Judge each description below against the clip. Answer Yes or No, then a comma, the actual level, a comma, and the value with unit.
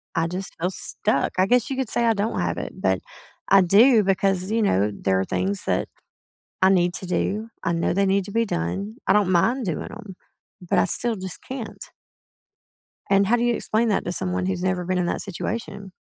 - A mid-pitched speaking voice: No, high, 195 Hz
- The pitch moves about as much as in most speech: Yes, average, 3.5 semitones